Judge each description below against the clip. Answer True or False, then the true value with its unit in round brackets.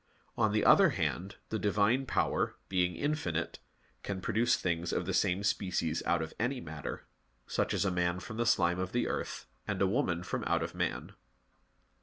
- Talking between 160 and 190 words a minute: True (185 wpm)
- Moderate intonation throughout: True (4.0 semitones)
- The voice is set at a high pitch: False (95 Hz)